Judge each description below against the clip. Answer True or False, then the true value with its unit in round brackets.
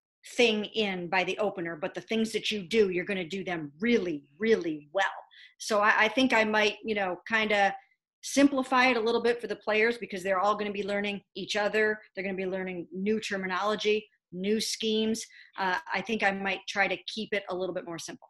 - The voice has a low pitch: False (205 Hz)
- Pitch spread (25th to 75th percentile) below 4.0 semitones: True (2.6 semitones)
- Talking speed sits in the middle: False (225 wpm)